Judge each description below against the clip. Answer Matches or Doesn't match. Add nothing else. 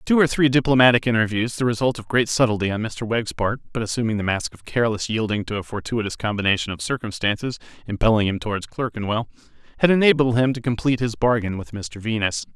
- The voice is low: Matches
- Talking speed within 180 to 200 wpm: Matches